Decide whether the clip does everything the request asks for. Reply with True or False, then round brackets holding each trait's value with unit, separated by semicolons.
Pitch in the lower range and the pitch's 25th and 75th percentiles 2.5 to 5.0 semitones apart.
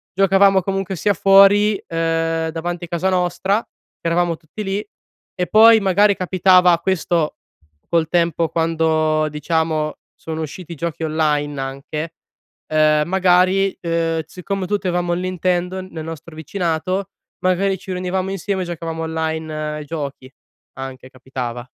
False (170 Hz; 2.9 semitones)